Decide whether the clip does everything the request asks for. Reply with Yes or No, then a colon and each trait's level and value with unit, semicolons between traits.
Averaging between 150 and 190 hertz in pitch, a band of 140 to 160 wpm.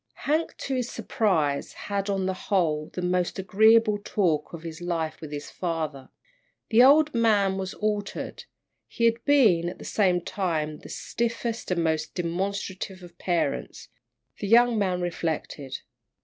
Yes: medium, 185 Hz; average, 155 wpm